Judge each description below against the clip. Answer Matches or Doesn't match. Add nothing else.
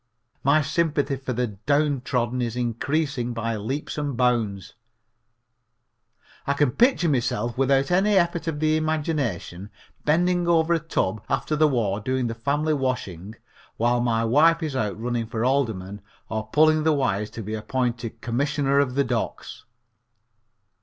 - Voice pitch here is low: Matches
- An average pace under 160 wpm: Matches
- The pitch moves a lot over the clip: Doesn't match